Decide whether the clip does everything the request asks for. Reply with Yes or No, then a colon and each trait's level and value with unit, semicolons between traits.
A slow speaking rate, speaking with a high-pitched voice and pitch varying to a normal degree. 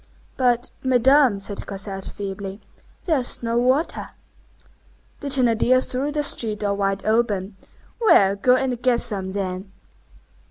Yes: slow, 130 wpm; high, 230 Hz; average, 4.4 semitones